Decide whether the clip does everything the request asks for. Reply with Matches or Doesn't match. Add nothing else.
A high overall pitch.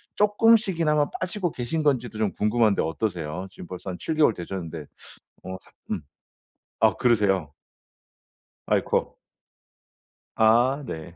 Doesn't match